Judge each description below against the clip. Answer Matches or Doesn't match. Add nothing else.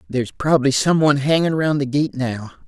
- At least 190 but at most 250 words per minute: Matches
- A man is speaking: Matches